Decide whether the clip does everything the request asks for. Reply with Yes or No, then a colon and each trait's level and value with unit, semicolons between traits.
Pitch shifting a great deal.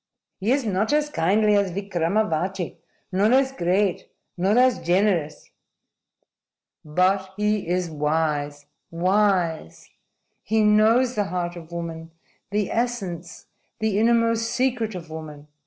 No: average, 4.4 semitones